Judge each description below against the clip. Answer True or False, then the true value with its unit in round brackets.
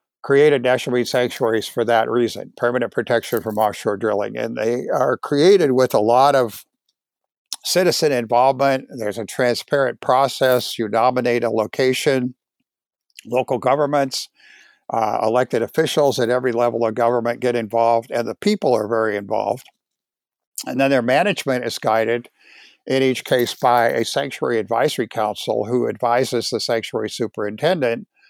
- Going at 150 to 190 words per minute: False (140 wpm)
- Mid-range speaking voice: False (125 Hz)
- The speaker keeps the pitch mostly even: True (2.3 semitones)